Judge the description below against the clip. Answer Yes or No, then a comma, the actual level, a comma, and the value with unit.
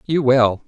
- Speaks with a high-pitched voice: No, low, 130 Hz